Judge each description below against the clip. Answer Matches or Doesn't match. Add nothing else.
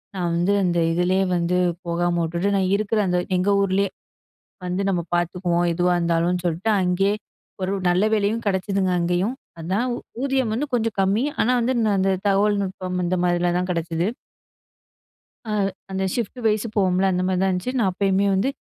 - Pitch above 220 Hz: Doesn't match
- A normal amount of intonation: Doesn't match